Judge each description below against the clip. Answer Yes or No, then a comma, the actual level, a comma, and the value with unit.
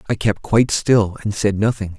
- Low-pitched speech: Yes, low, 105 Hz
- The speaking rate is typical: No, fast, 210 wpm